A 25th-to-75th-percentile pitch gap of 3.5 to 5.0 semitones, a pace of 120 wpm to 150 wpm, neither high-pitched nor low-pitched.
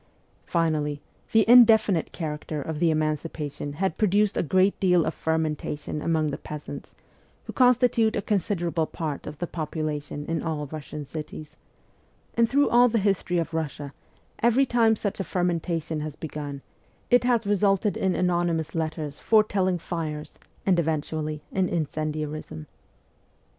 Yes: average, 4.6 semitones; average, 140 wpm; medium, 165 Hz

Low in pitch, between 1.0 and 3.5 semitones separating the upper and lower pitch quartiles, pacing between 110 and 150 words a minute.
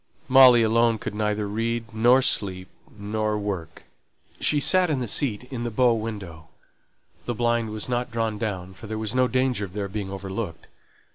No: low, 110 Hz; average, 2.8 semitones; average, 180 wpm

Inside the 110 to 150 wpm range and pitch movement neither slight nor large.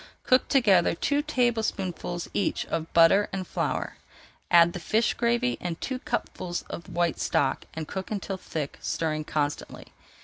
No: average, 145 wpm; wide, 6.0 semitones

